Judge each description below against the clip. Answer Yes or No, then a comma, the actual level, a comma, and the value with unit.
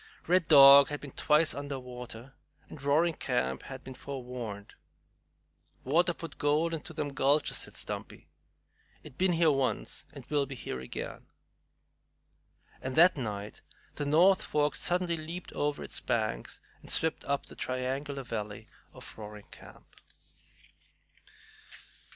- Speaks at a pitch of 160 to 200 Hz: No, medium, 140 Hz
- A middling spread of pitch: Yes, average, 3.7 semitones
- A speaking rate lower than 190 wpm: Yes, average, 140 wpm